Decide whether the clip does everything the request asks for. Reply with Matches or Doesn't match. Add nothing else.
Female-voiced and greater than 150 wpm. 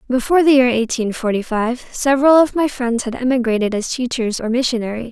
Matches